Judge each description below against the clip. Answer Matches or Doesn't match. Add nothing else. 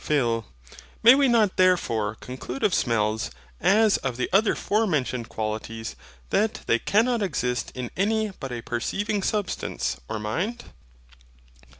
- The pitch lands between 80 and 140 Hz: Doesn't match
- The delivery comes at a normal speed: Doesn't match